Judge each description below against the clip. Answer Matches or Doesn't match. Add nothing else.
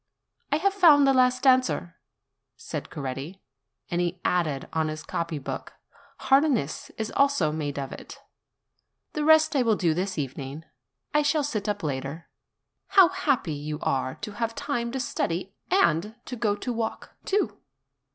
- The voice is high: Matches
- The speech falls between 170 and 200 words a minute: Doesn't match